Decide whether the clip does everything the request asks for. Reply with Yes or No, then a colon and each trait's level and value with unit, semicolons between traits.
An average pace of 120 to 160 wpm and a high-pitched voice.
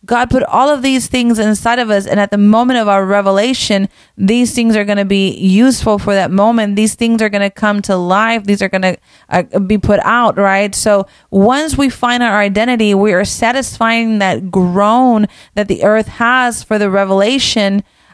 No: average, 200 wpm; high, 210 Hz